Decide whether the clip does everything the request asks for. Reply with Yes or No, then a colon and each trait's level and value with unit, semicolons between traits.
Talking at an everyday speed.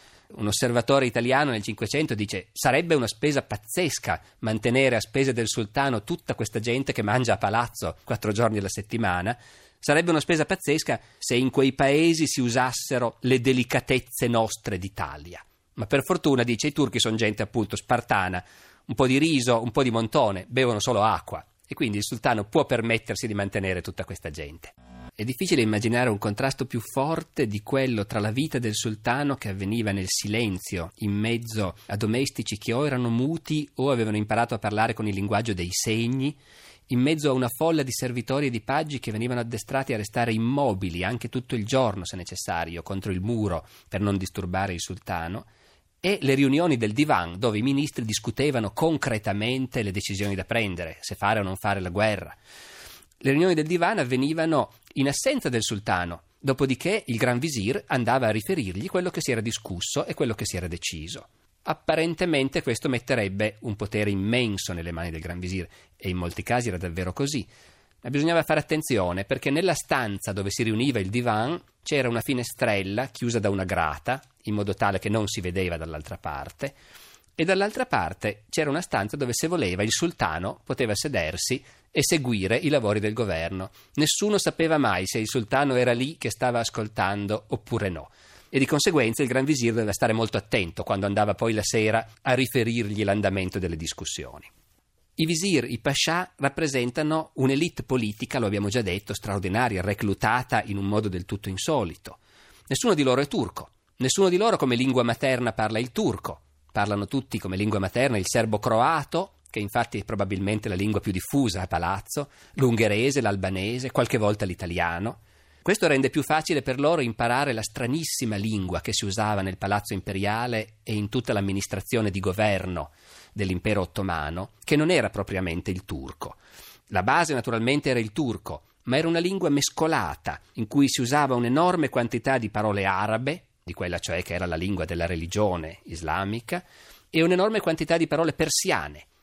No: fast, 175 wpm